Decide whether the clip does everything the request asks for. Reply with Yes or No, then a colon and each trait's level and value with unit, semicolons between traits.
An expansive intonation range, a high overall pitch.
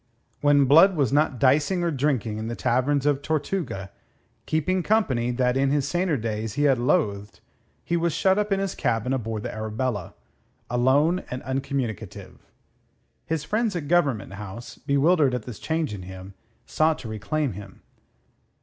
No: wide, 5.8 semitones; low, 135 Hz